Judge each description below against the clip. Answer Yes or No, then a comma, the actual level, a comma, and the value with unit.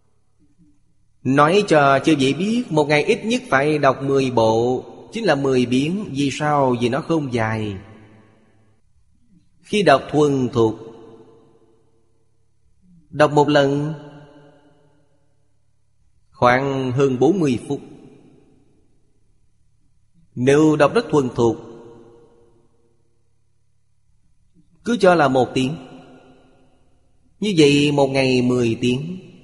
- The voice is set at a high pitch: No, low, 130 Hz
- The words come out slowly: Yes, slow, 105 wpm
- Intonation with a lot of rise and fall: No, average, 4.3 semitones